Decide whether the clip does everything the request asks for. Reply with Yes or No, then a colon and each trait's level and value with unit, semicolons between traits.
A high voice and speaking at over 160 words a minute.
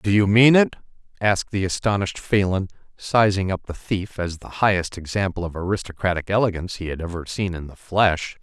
No: very low, 95 Hz; average, 185 wpm